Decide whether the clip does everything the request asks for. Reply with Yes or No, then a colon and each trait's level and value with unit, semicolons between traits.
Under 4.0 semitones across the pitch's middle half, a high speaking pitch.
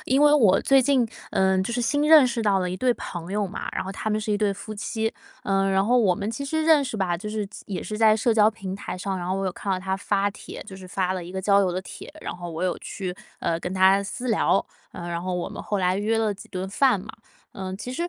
Yes: average, 3.1 semitones; high, 200 Hz